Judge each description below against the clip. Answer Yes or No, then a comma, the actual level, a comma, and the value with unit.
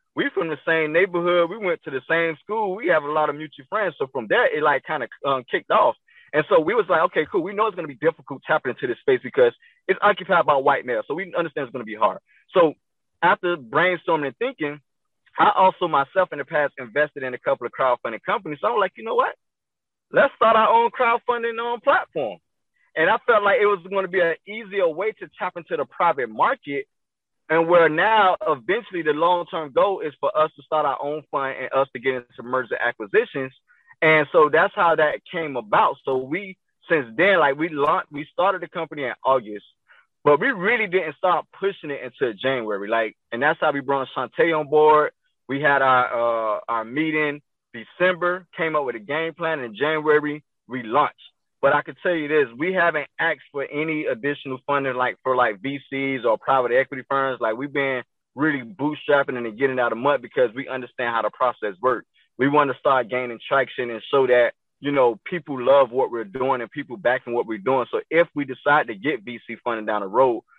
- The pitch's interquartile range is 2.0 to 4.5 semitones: No, wide, 5.4 semitones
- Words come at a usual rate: No, fast, 215 wpm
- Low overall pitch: No, medium, 150 Hz